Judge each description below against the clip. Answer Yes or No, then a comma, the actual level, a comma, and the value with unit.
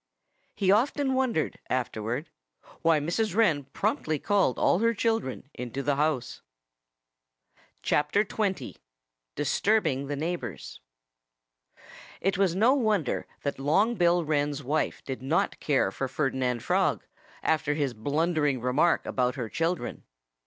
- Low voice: No, medium, 155 Hz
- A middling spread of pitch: No, wide, 6.2 semitones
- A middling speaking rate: No, slow, 120 wpm